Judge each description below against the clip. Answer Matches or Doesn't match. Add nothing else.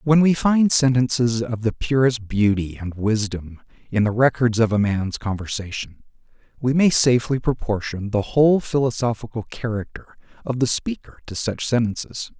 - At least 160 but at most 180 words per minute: Doesn't match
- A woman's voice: Doesn't match